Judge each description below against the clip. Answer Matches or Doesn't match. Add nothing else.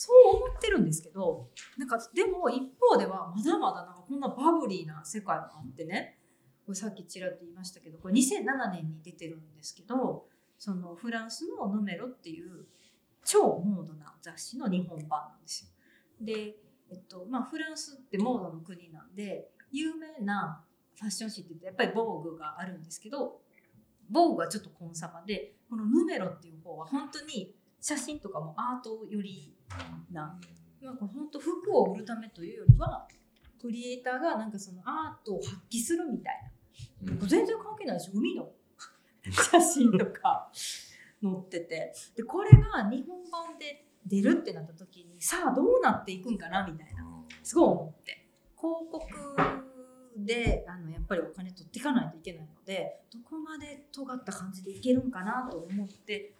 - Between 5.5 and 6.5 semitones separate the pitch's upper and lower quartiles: Doesn't match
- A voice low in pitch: Doesn't match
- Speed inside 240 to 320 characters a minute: Doesn't match